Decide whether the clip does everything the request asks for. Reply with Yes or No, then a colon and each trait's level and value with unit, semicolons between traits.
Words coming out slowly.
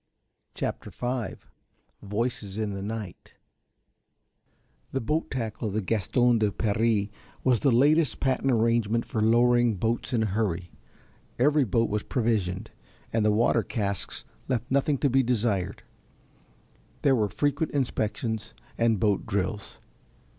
Yes: slow, 130 wpm